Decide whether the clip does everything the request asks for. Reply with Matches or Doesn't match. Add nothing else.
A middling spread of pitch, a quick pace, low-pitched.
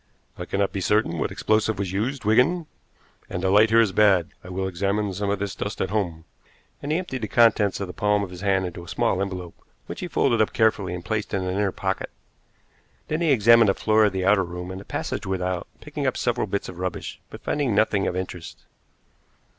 Matches